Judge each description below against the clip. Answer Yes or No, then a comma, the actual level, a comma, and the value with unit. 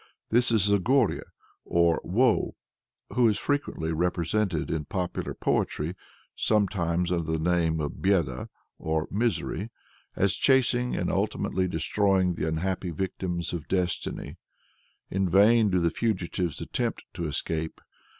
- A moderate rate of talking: No, slow, 125 wpm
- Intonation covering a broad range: No, average, 3.8 semitones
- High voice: No, very low, 90 Hz